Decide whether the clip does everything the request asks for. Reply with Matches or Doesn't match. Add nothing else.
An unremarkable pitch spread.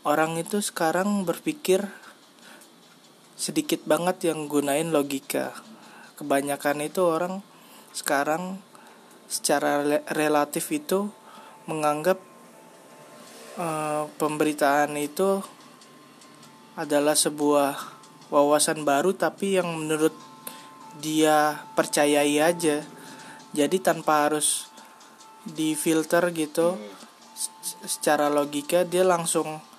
Matches